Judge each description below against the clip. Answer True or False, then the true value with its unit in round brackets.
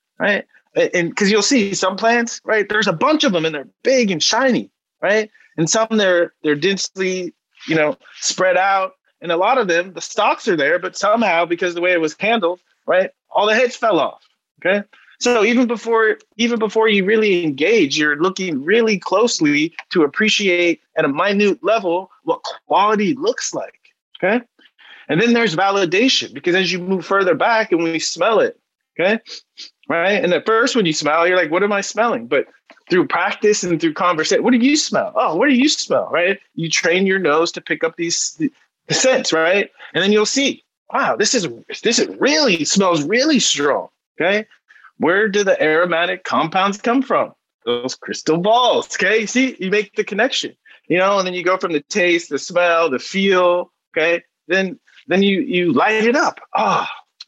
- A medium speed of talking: True (190 wpm)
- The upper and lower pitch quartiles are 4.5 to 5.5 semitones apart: True (5.1 semitones)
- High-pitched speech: True (195 Hz)